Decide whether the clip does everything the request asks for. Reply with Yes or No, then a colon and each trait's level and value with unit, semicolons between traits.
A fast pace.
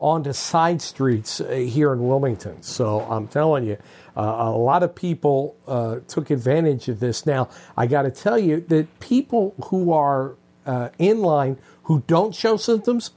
No: average, 170 wpm